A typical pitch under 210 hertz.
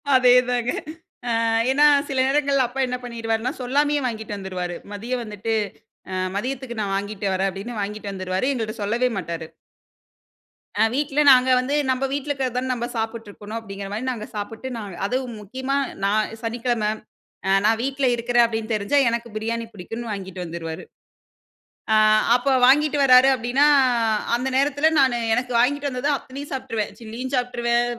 No: high, 240 Hz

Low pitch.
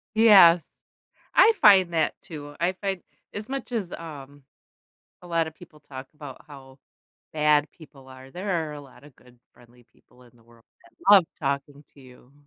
No: medium, 150 Hz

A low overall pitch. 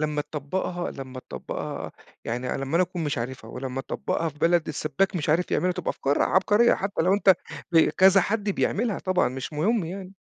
No: medium, 165 Hz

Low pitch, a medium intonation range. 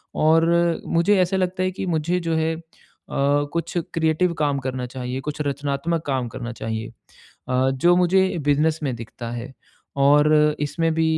No: medium, 155 Hz; average, 4.2 semitones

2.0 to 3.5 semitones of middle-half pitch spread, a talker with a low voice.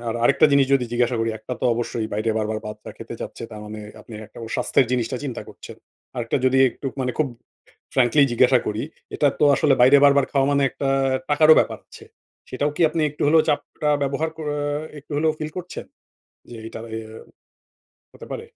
No: average, 4.0 semitones; low, 130 Hz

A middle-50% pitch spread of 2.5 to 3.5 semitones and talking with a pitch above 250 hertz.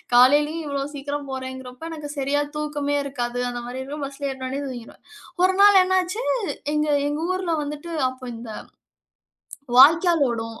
Yes: average, 2.8 semitones; very high, 285 Hz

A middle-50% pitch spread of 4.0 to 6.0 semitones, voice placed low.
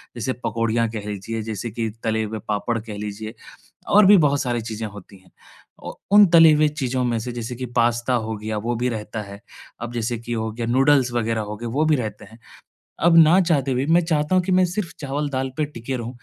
Yes: average, 4.5 semitones; low, 120 Hz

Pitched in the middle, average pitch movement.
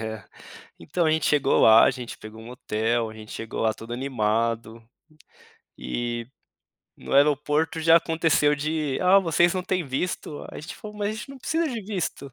No: medium, 145 Hz; wide, 6.6 semitones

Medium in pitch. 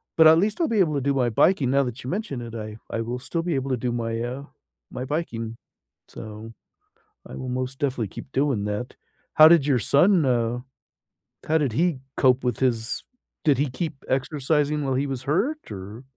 No: low, 130 Hz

